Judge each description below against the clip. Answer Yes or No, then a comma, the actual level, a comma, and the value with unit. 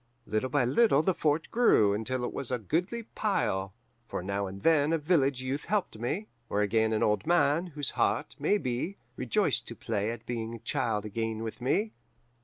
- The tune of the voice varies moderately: No, wide, 6.5 semitones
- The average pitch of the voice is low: Yes, low, 130 Hz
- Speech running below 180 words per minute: No, average, 185 wpm